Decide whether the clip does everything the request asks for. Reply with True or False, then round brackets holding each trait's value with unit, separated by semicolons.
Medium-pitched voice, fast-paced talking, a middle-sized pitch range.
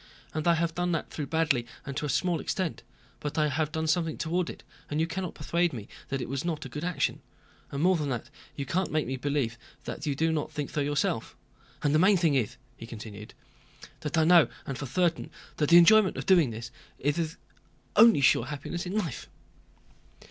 True (155 Hz; 220 wpm; 3.5 semitones)